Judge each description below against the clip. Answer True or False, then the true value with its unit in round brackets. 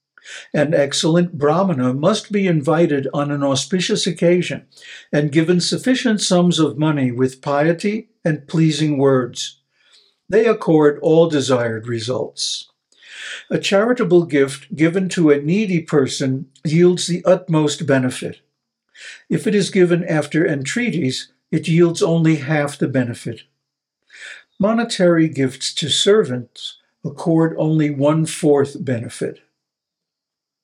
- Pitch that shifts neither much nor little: True (4.0 semitones)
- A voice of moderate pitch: True (160 Hz)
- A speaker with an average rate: False (115 wpm)